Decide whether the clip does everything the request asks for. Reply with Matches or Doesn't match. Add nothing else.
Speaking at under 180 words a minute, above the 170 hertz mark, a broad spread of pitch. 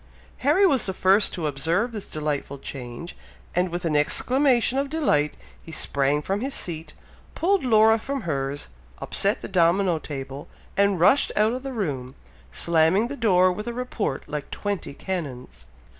Matches